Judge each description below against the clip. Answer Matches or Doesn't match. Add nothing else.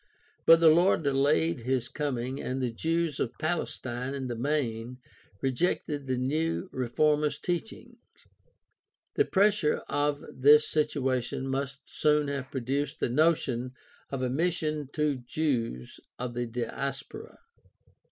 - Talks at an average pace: Doesn't match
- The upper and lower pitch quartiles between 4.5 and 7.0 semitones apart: Doesn't match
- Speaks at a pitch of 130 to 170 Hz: Matches